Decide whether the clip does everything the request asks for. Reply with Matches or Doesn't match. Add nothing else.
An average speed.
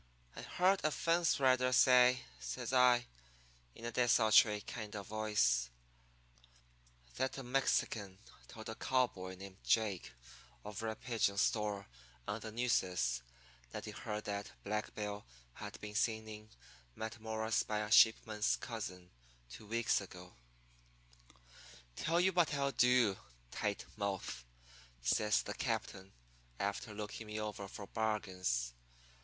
Doesn't match